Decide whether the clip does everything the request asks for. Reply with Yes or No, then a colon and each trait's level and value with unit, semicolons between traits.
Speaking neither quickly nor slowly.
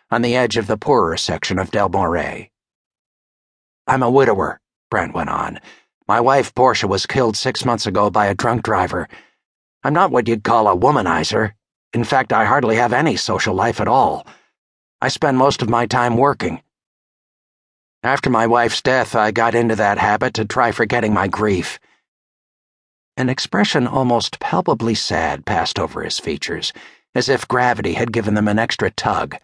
Yes: average, 170 wpm